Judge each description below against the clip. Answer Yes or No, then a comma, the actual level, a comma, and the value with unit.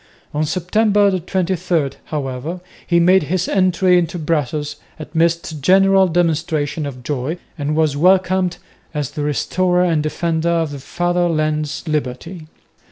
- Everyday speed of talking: No, slow, 130 wpm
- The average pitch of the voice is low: No, medium, 165 Hz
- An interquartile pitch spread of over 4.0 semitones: No, average, 3.3 semitones